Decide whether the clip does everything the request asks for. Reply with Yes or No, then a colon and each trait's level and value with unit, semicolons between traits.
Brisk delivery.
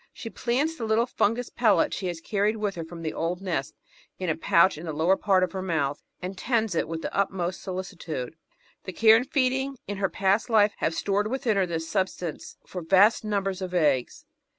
Yes: fast, 210 wpm